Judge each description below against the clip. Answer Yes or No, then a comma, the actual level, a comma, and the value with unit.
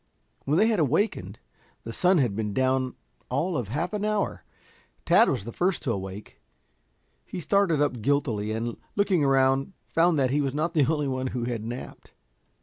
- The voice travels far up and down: Yes, wide, 6.0 semitones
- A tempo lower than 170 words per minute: No, average, 175 wpm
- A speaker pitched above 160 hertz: No, low, 135 Hz